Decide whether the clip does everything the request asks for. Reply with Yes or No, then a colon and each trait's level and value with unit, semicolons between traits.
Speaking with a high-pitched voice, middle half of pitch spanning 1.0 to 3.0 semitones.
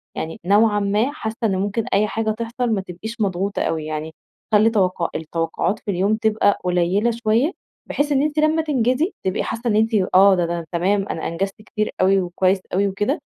No: high, 205 Hz; average, 3.4 semitones